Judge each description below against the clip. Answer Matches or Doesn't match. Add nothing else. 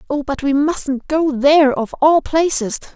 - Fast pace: Doesn't match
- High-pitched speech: Matches